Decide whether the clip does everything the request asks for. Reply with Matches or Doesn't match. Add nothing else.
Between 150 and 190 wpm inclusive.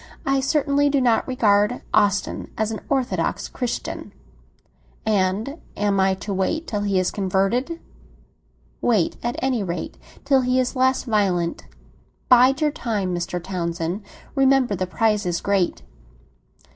Doesn't match